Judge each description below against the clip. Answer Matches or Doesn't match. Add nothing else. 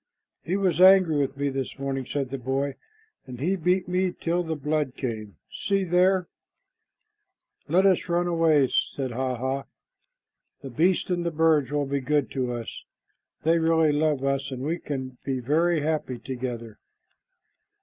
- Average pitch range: Matches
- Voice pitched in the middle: Matches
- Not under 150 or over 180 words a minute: Matches